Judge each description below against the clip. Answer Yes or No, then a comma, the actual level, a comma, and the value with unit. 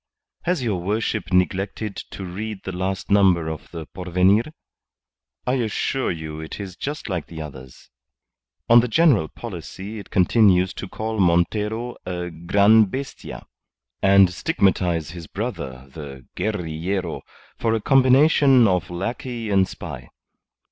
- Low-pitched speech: Yes, very low, 95 Hz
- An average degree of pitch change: Yes, average, 4.3 semitones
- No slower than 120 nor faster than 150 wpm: Yes, slow, 135 wpm